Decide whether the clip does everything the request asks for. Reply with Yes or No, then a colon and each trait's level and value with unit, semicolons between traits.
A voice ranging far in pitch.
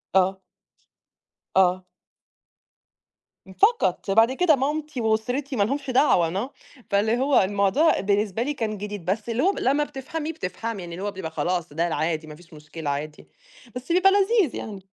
Yes: wide, 7.2 semitones